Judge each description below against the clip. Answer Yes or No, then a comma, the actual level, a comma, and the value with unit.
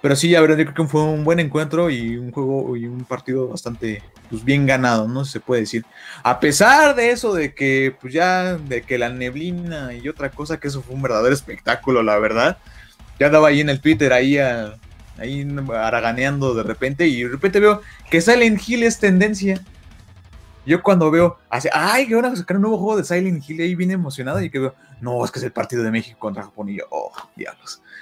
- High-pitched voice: No, medium, 140 Hz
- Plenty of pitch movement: Yes, wide, 6.1 semitones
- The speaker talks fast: Yes, fast, 225 wpm